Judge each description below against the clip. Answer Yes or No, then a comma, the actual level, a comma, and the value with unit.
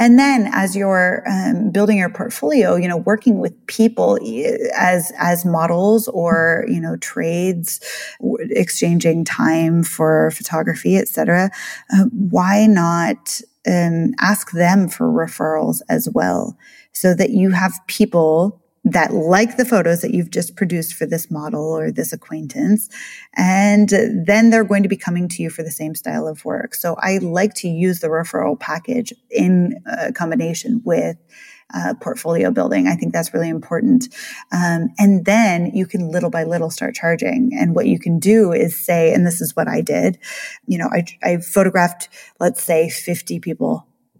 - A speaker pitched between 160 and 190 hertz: Yes, medium, 185 Hz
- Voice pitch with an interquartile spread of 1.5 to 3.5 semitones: No, average, 4.9 semitones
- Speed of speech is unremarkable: Yes, average, 165 wpm